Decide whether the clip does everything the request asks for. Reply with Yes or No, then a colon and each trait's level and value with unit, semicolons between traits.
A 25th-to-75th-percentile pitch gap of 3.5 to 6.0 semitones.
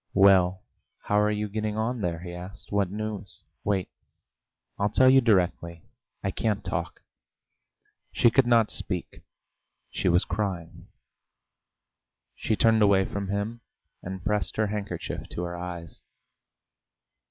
No: average, 3.0 semitones